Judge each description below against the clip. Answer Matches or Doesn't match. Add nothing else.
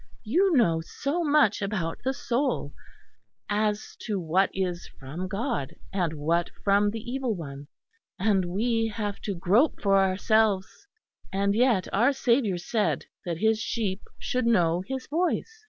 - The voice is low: Doesn't match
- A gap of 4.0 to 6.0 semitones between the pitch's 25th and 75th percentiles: Matches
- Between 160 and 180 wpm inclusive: Doesn't match